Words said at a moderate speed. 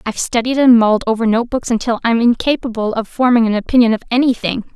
Yes: average, 190 wpm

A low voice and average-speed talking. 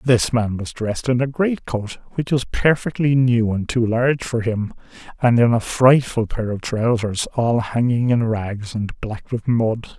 Yes: low, 120 Hz; average, 190 wpm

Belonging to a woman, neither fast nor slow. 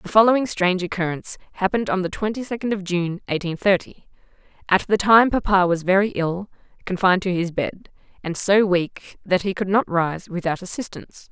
Yes: female; average, 175 wpm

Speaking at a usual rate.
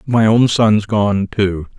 Yes: average, 170 wpm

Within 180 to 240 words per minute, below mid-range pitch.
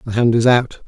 No: fast, 275 wpm; low, 120 Hz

